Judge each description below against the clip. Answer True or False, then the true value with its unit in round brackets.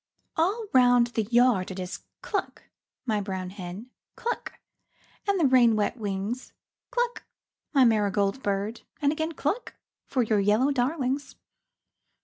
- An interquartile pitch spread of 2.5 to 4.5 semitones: False (5.5 semitones)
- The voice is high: True (240 Hz)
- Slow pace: True (130 wpm)